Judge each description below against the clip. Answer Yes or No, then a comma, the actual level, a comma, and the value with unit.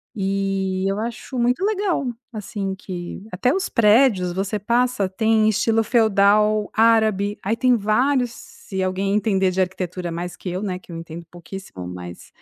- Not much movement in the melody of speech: No, average, 3.3 semitones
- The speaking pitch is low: No, high, 200 Hz